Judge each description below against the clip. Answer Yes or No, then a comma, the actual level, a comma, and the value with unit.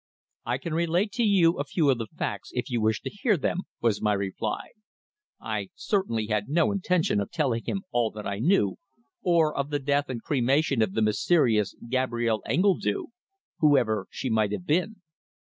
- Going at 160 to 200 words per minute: Yes, average, 180 wpm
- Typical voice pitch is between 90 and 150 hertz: Yes, low, 135 Hz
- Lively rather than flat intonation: Yes, wide, 7.5 semitones